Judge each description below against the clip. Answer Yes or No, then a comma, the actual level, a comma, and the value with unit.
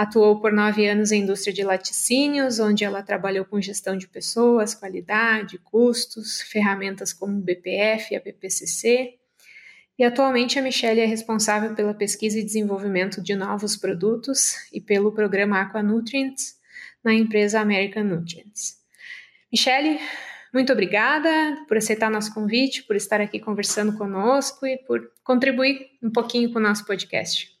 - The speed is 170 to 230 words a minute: No, average, 145 wpm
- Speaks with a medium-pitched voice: No, high, 215 Hz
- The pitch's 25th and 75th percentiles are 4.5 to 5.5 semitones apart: No, average, 3.2 semitones